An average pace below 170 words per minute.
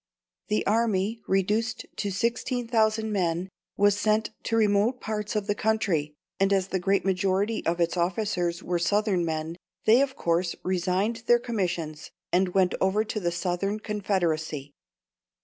Yes: average, 150 wpm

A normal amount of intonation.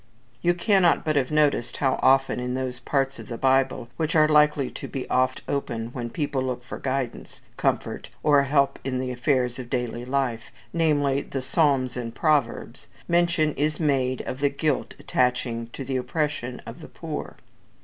Yes: average, 3.0 semitones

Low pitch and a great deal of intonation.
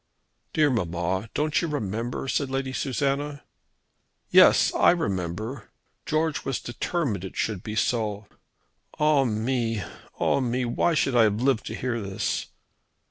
No: low, 120 Hz; average, 4.6 semitones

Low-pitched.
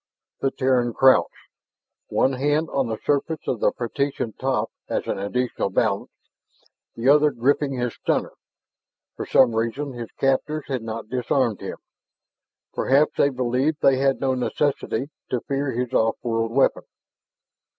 Yes: low, 130 Hz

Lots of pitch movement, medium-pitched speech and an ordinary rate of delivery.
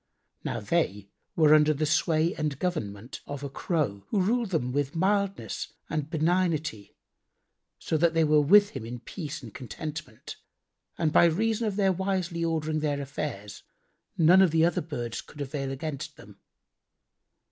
No: average, 3.7 semitones; medium, 155 Hz; average, 160 wpm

